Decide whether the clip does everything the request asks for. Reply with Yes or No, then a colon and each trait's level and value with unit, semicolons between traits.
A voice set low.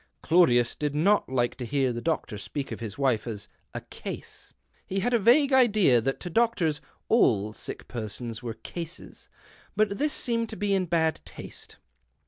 No: medium, 160 Hz